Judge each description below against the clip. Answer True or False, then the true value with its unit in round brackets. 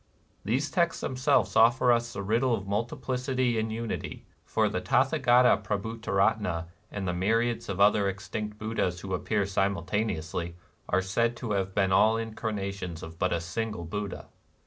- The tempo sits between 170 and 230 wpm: False (155 wpm)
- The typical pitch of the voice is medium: False (105 Hz)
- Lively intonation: False (3.5 semitones)